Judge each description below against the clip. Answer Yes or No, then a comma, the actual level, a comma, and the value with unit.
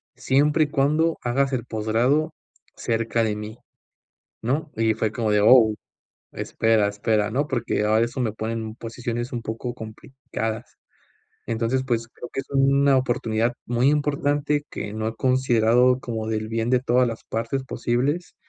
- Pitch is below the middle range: Yes, low, 120 Hz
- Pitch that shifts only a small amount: No, average, 3.2 semitones